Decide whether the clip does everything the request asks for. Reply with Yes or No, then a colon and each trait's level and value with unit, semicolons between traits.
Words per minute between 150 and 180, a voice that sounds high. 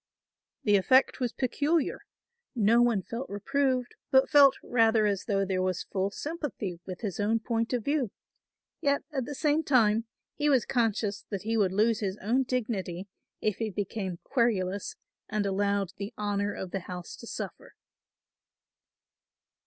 Yes: average, 155 wpm; high, 220 Hz